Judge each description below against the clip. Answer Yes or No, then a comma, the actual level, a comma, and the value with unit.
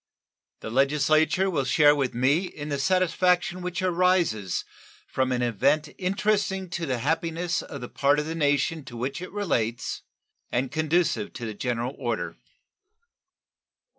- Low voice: No, medium, 150 Hz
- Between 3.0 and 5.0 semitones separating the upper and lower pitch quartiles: No, wide, 5.5 semitones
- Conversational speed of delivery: Yes, average, 145 wpm